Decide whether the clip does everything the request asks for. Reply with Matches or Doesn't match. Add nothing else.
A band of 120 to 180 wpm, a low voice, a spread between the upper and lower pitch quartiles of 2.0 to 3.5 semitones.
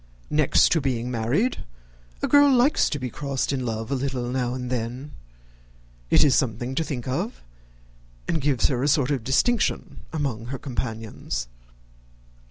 Matches